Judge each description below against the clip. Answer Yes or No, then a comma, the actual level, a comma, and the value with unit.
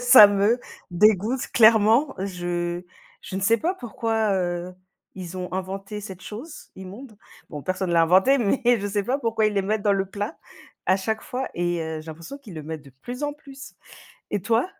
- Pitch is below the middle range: No, high, 200 Hz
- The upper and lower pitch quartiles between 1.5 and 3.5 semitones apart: No, average, 4.1 semitones